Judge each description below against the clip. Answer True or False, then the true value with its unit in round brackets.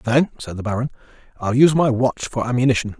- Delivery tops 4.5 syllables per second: True (6.5 syllables/s)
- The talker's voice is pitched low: True (125 Hz)